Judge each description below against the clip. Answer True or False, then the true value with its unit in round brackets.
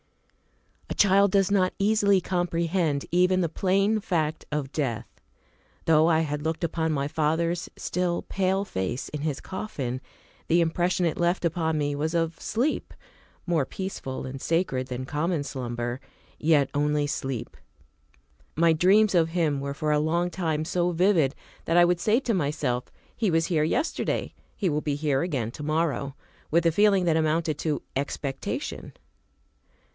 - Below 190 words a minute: True (160 wpm)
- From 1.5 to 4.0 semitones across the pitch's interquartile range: True (3.5 semitones)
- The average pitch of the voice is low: False (160 Hz)